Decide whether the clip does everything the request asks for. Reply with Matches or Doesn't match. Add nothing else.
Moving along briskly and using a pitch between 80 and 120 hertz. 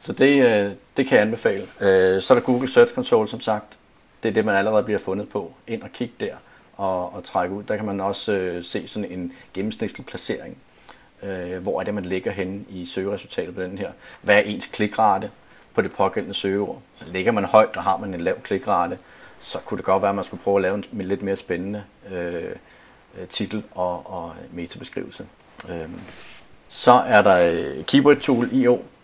Doesn't match